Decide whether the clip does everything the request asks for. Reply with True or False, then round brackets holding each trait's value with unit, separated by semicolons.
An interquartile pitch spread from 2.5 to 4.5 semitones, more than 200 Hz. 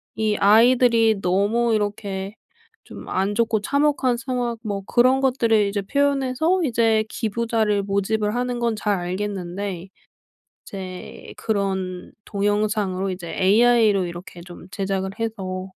True (3.3 semitones; 210 Hz)